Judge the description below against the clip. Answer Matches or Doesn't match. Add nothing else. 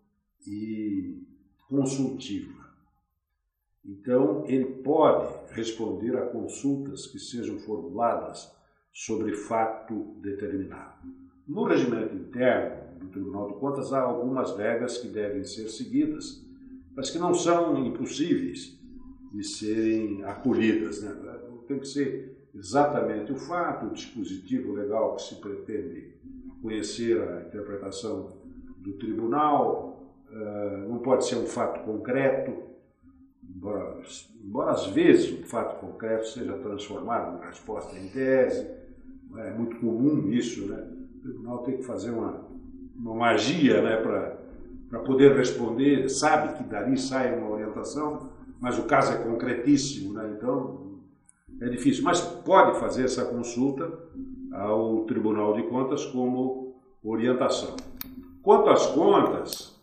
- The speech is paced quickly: Doesn't match